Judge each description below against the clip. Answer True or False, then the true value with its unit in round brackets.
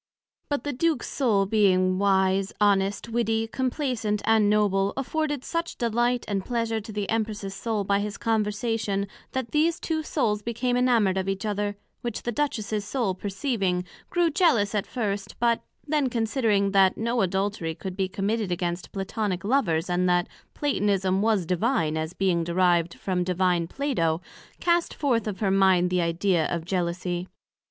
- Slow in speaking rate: False (160 wpm)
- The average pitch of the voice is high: True (205 Hz)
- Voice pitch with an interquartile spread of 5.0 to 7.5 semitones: False (3.9 semitones)